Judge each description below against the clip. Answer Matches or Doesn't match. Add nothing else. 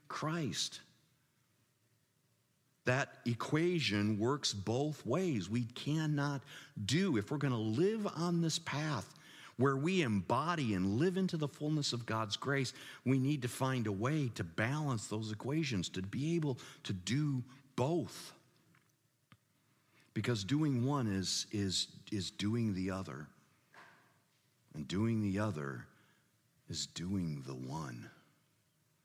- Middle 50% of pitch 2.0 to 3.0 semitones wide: Doesn't match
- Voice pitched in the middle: Doesn't match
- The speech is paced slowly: Matches